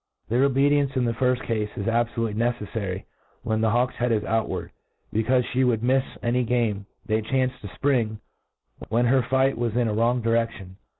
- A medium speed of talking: Yes, average, 180 wpm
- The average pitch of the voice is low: Yes, low, 120 Hz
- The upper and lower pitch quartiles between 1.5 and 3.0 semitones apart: Yes, narrow, 2.4 semitones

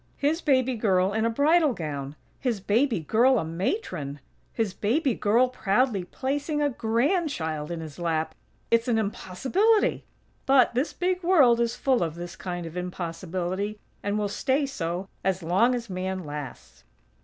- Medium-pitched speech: No, high, 215 Hz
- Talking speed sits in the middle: Yes, average, 155 wpm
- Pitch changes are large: Yes, wide, 7.0 semitones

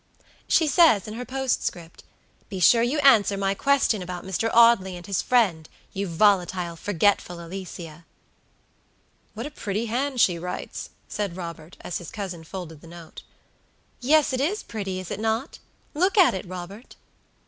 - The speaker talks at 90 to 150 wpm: No, average, 160 wpm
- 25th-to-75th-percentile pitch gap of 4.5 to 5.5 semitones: Yes, average, 5.2 semitones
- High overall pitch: Yes, high, 195 Hz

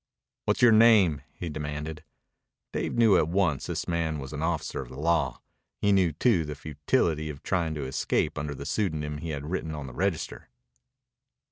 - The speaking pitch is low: Yes, very low, 80 Hz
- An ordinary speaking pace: Yes, average, 180 wpm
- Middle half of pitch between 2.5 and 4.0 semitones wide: Yes, average, 3.2 semitones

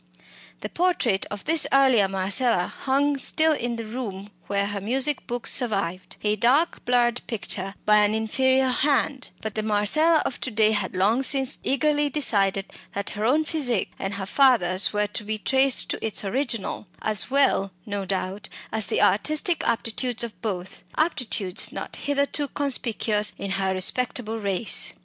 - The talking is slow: No, average, 160 wpm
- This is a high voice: Yes, high, 225 Hz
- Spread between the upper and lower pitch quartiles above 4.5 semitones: Yes, average, 5.0 semitones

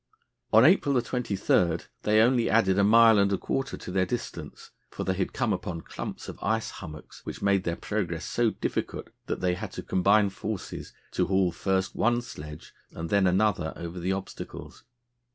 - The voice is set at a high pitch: No, low, 100 Hz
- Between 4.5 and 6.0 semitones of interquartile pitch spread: No, average, 3.5 semitones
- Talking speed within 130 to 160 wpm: No, average, 180 wpm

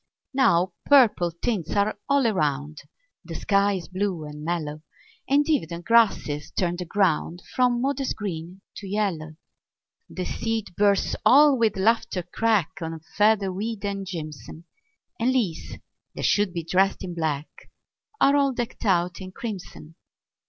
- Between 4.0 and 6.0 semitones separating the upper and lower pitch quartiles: Yes, average, 5.0 semitones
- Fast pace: No, average, 145 wpm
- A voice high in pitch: Yes, high, 195 Hz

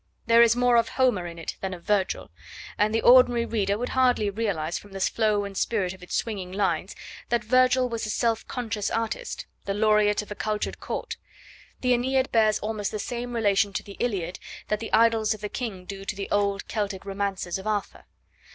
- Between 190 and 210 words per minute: Yes, fast, 205 wpm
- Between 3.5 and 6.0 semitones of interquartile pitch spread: No, average, 2.8 semitones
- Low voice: No, high, 215 Hz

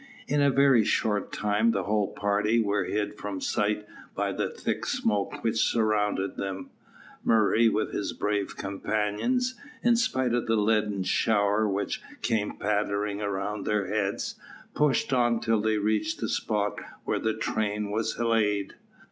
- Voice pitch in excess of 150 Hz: No, low, 105 Hz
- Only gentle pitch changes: Yes, narrow, 1.7 semitones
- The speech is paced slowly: No, average, 150 wpm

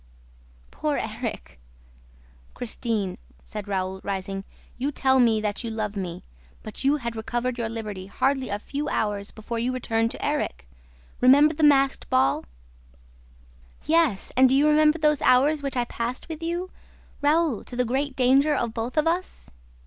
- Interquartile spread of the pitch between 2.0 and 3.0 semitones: No, average, 5.1 semitones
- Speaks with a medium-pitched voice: No, very high, 250 Hz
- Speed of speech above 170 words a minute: No, average, 160 wpm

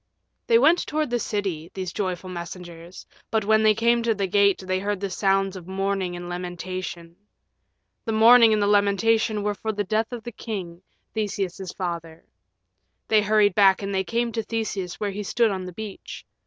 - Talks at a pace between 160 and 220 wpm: Yes, average, 185 wpm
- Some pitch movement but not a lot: Yes, average, 3.0 semitones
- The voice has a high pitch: Yes, high, 200 Hz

